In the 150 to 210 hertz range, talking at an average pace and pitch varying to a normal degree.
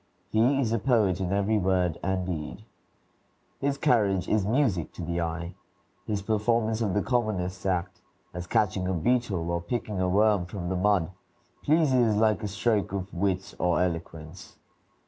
No: low, 100 Hz; average, 165 wpm; average, 3.6 semitones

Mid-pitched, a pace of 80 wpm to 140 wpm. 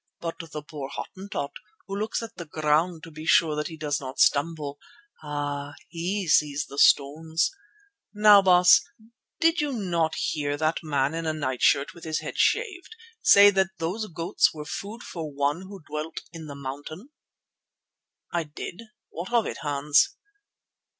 No: medium, 160 Hz; average, 165 wpm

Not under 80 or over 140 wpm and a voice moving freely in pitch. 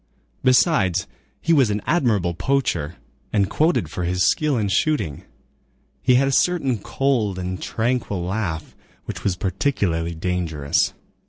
Yes: slow, 135 wpm; wide, 7.1 semitones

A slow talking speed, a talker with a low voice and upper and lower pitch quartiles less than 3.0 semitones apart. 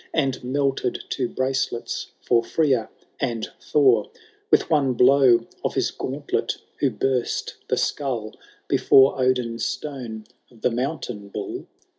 Yes: slow, 125 wpm; low, 130 Hz; narrow, 2.6 semitones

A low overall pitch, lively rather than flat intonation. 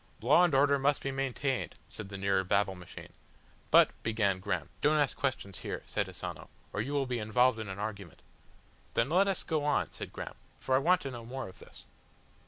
Yes: low, 125 Hz; wide, 5.8 semitones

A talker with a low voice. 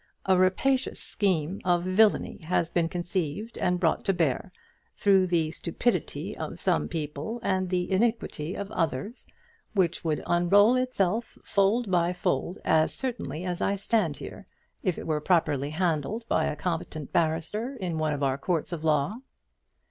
No: medium, 180 Hz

